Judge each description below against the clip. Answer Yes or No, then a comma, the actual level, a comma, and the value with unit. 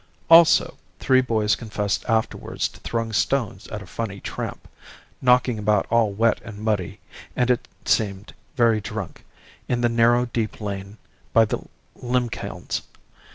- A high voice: No, low, 115 Hz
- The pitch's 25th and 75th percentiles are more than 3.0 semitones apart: No, narrow, 2.4 semitones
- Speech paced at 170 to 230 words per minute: No, average, 140 wpm